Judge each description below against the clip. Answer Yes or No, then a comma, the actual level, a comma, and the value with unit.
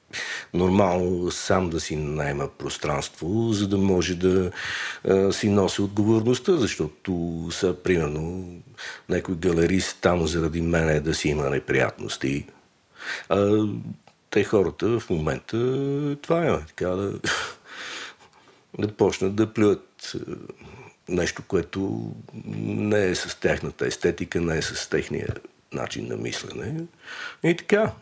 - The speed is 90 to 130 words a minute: Yes, average, 120 wpm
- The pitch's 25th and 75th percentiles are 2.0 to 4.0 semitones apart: No, average, 4.4 semitones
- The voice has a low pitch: Yes, very low, 95 Hz